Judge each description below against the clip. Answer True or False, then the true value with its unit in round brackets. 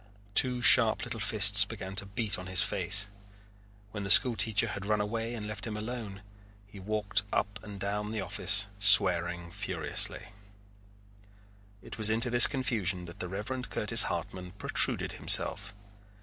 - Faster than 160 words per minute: False (155 wpm)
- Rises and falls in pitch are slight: True (2.3 semitones)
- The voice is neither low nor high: False (105 Hz)